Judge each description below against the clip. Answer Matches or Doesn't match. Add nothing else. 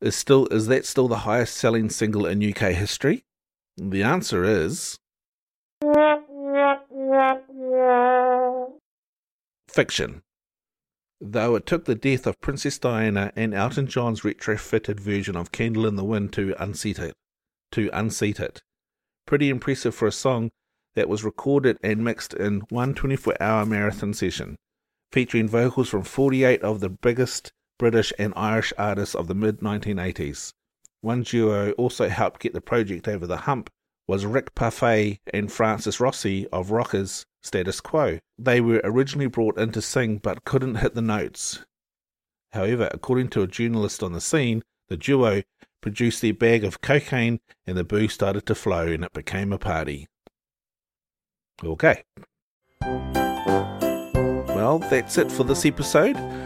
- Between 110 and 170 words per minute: Matches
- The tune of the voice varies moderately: Matches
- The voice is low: Matches